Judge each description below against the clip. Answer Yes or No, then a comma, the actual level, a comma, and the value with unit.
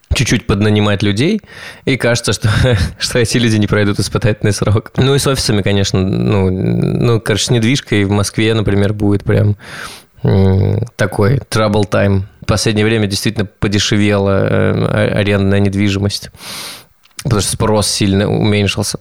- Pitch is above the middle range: No, low, 105 Hz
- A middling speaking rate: Yes, average, 135 wpm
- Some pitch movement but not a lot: No, narrow, 2.1 semitones